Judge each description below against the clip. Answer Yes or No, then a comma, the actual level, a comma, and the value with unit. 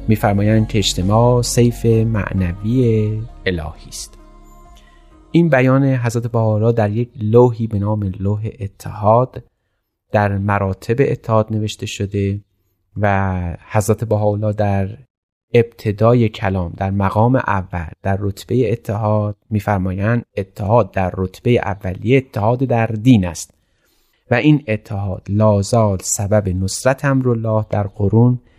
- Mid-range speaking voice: No, low, 105 Hz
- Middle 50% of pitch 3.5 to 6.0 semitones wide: No, average, 3.1 semitones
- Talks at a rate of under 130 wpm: Yes, average, 110 wpm